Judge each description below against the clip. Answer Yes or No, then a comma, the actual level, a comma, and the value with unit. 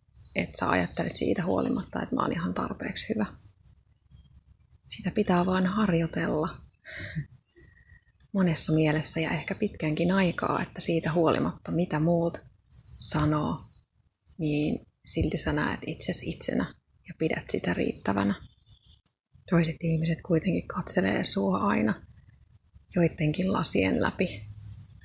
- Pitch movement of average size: Yes, average, 3.0 semitones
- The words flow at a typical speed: Yes, average, 110 wpm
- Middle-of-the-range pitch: Yes, medium, 160 Hz